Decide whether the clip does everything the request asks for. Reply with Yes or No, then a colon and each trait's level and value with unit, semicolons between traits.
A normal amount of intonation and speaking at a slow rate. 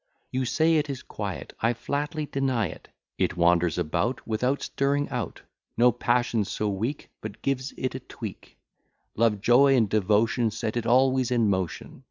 No: average, 3.9 semitones; average, 165 wpm